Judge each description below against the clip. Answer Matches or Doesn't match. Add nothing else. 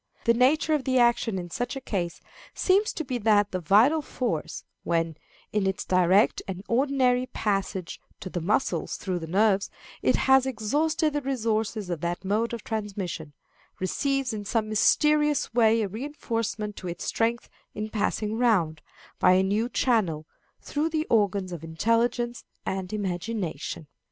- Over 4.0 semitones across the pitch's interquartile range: Matches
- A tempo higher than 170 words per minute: Doesn't match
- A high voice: Matches